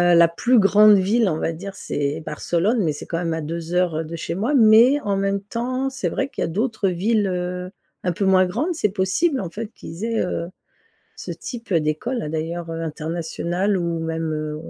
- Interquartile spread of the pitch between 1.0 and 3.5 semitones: No, average, 4.9 semitones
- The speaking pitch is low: No, medium, 185 Hz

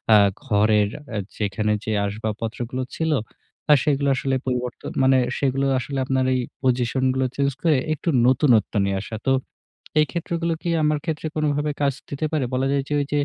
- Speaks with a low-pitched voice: Yes, low, 130 Hz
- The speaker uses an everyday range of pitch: Yes, average, 3.9 semitones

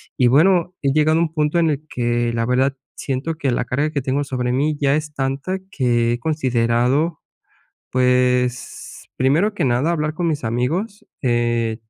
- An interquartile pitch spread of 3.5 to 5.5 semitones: Yes, average, 3.9 semitones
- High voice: No, low, 135 Hz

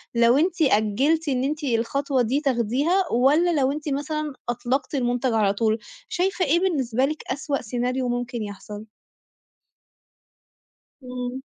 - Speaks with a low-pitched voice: No, very high, 260 Hz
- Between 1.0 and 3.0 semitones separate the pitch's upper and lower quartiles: No, average, 3.8 semitones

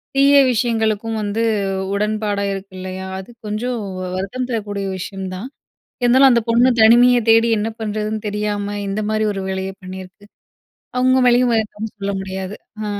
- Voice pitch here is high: Yes, high, 215 Hz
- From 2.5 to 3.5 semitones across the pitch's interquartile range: Yes, average, 3.0 semitones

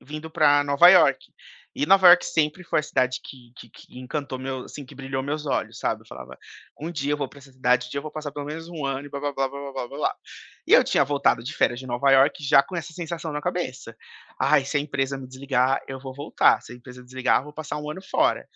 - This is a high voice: No, medium, 140 Hz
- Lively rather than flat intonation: No, narrow, 2.4 semitones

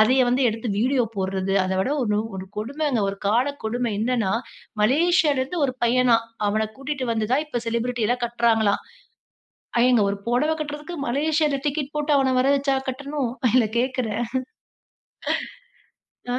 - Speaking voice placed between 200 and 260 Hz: Yes, very high, 250 Hz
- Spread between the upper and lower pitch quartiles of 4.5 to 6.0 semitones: No, average, 3.8 semitones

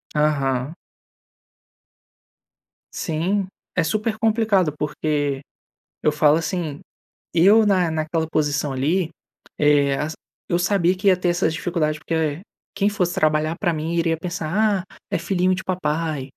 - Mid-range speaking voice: Yes, medium, 165 Hz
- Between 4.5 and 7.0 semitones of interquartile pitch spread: No, average, 3.4 semitones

